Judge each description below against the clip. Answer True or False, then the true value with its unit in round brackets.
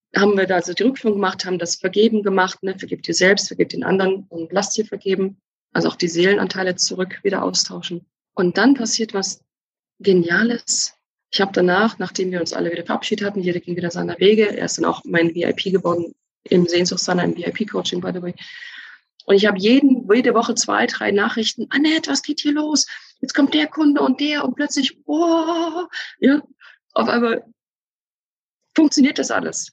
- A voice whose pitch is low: False (205 Hz)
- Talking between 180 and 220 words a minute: True (185 wpm)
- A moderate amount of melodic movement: False (6.4 semitones)